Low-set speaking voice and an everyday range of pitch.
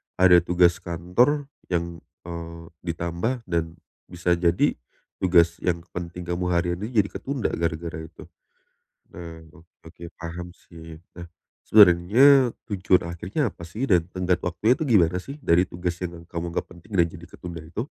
No: very low, 85 Hz; narrow, 1.8 semitones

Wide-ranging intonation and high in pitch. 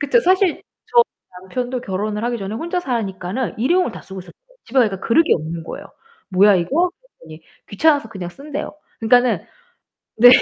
Yes: wide, 6.9 semitones; high, 235 Hz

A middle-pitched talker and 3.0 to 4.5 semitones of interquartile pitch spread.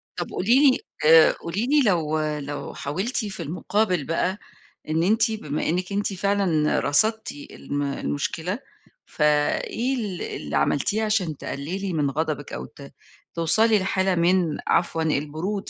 No: medium, 175 Hz; average, 5.1 semitones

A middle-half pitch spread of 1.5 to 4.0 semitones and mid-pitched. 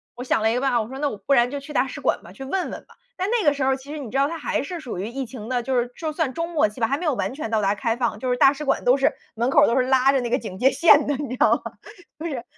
No: average, 3.2 semitones; very high, 265 Hz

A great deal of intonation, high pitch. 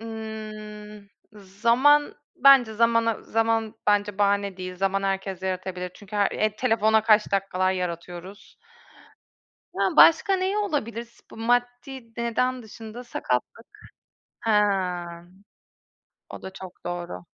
No: average, 3.3 semitones; high, 215 Hz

